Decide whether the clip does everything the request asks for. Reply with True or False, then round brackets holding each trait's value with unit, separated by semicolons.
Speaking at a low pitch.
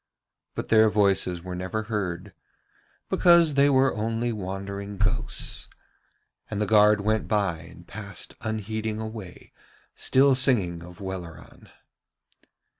True (105 Hz)